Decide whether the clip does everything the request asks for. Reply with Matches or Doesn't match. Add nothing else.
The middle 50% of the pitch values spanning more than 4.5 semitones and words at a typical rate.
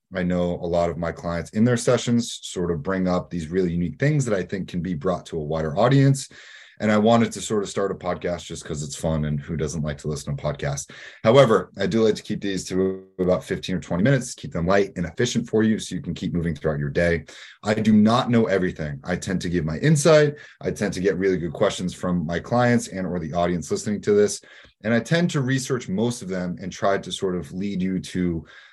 Doesn't match